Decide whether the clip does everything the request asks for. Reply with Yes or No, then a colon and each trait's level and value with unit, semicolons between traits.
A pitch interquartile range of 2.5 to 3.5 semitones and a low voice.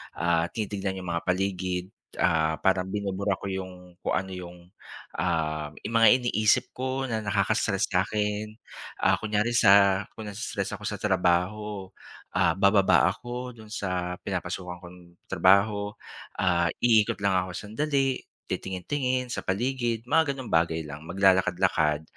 Yes: average, 3.2 semitones; very low, 95 Hz